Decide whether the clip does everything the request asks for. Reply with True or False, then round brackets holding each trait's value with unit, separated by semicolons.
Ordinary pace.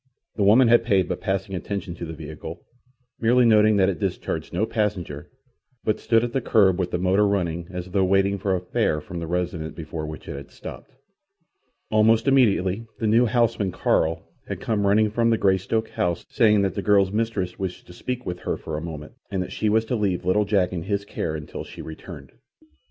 False (210 wpm)